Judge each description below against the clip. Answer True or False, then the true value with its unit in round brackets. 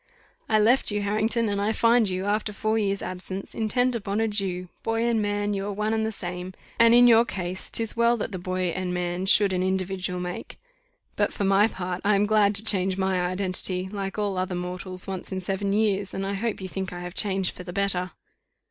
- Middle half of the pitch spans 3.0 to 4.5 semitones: False (2.5 semitones)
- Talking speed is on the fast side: True (225 wpm)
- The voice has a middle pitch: False (195 Hz)